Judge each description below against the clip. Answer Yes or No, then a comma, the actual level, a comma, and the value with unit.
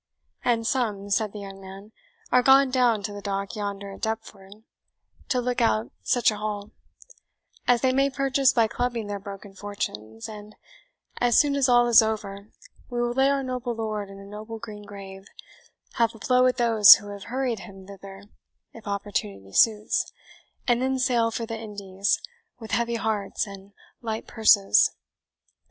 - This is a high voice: Yes, high, 215 Hz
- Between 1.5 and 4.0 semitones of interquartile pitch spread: Yes, average, 3.3 semitones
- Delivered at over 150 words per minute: Yes, average, 170 wpm